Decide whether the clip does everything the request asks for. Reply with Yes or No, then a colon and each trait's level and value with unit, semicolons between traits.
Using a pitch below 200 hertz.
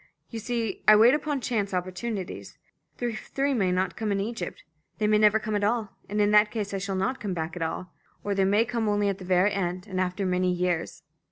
No: high, 205 Hz